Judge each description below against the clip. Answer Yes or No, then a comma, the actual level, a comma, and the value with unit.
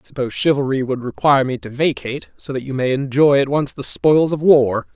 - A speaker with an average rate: No, fast, 230 wpm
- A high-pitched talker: No, low, 130 Hz